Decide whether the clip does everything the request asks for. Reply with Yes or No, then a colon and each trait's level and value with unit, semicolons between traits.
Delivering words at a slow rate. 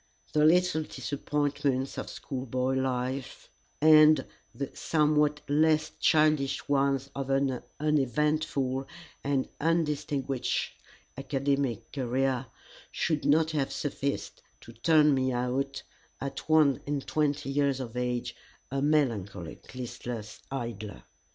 Yes: slow, 105 wpm